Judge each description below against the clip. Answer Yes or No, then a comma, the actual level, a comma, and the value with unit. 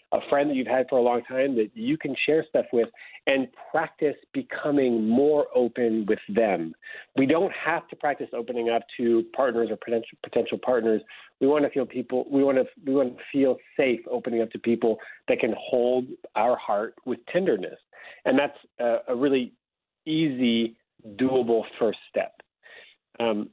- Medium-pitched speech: No, low, 125 Hz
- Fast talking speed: No, average, 175 wpm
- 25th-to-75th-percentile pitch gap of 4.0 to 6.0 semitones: No, average, 3.1 semitones